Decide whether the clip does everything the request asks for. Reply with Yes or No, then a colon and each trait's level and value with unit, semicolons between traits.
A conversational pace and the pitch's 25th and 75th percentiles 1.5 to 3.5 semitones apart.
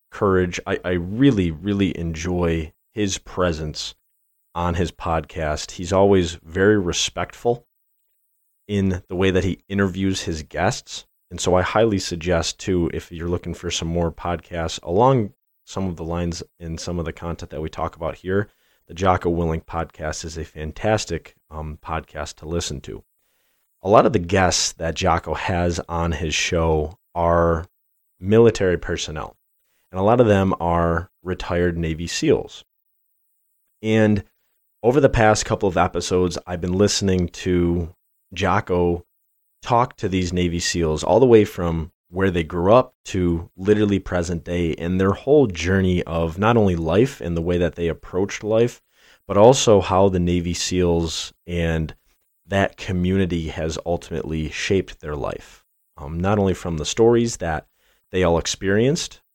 Yes: average, 155 wpm; narrow, 2.6 semitones